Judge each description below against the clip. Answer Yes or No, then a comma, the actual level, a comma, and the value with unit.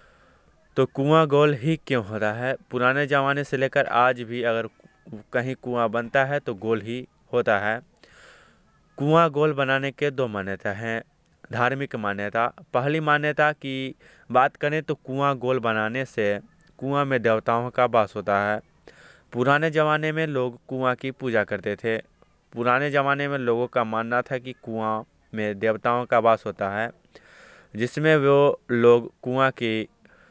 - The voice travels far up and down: No, average, 3.6 semitones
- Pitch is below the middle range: Yes, low, 125 Hz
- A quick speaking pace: No, average, 155 wpm